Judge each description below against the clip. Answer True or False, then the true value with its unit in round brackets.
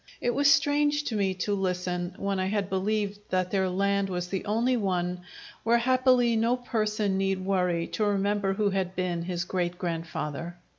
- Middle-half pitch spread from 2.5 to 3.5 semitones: True (3.0 semitones)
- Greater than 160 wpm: True (180 wpm)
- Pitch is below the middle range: False (195 Hz)